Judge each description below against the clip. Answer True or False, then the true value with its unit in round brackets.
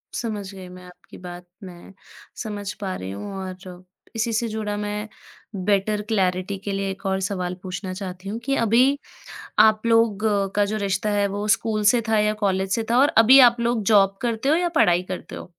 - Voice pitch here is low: False (205 Hz)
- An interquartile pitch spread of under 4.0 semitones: True (2.8 semitones)